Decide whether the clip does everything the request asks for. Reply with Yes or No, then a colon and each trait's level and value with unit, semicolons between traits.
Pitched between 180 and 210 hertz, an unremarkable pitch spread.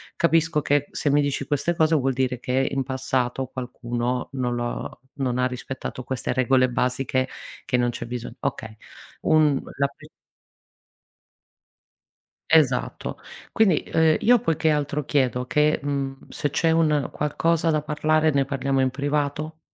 No: medium, 140 Hz; average, 3.0 semitones